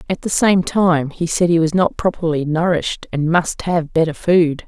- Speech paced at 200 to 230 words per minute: Yes, fast, 205 wpm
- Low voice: No, medium, 165 Hz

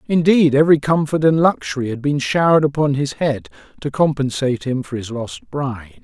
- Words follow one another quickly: No, average, 180 wpm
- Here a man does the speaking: Yes, male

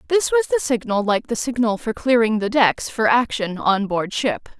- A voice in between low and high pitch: No, high, 230 Hz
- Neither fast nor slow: No, fast, 210 wpm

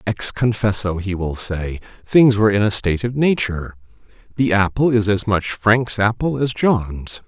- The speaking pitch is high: No, low, 105 Hz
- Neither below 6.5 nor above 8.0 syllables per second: No, 4.6 syllables/s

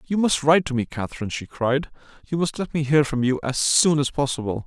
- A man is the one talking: Yes, male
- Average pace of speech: No, fast, 245 wpm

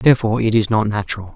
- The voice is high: No, low, 110 Hz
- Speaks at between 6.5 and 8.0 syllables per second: Yes, 7.7 syllables/s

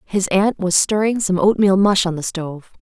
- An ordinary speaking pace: No, fast, 210 wpm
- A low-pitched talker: No, high, 190 Hz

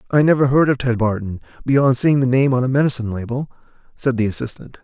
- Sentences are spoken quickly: Yes, fast, 210 wpm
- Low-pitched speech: Yes, low, 125 Hz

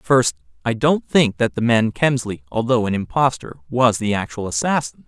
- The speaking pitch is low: Yes, low, 120 Hz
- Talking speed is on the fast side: No, average, 175 wpm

